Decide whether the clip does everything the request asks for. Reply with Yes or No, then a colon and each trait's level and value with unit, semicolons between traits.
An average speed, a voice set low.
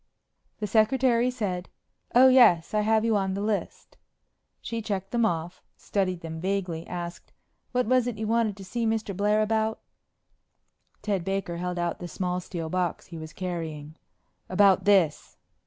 No: average, 160 wpm; high, 195 Hz